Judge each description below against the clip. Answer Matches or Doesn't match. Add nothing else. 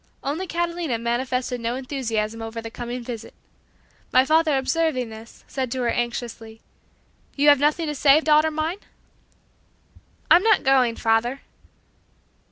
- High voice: Matches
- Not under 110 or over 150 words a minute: Matches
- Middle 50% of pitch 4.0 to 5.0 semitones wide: Matches